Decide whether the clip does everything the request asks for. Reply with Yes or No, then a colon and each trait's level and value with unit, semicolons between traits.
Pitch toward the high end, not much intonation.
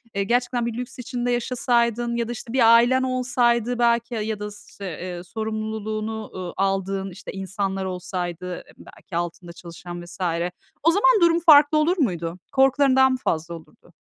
No: high, 220 Hz; average, 4.7 semitones